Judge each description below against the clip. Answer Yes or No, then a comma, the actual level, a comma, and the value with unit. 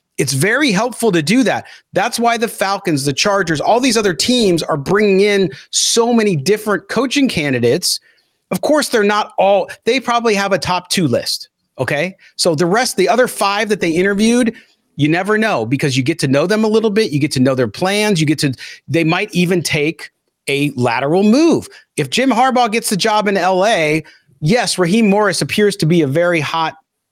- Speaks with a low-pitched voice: No, high, 195 Hz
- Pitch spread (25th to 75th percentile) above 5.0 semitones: Yes, wide, 5.4 semitones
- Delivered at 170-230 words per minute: Yes, average, 200 wpm